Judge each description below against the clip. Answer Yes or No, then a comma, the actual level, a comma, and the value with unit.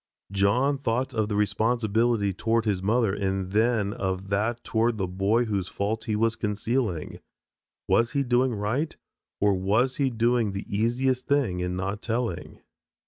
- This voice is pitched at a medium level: No, low, 110 Hz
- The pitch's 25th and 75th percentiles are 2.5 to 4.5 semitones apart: Yes, average, 3.3 semitones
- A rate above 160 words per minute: No, average, 155 wpm